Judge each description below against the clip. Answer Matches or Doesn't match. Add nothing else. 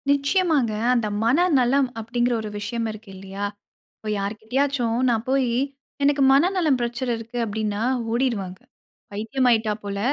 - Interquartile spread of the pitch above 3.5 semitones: Matches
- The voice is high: Matches